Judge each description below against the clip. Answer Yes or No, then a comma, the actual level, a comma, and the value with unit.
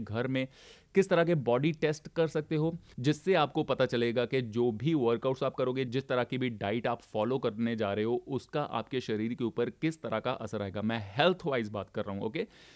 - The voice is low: Yes, low, 125 Hz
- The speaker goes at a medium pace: No, fast, 225 wpm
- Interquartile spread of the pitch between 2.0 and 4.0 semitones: No, average, 4.7 semitones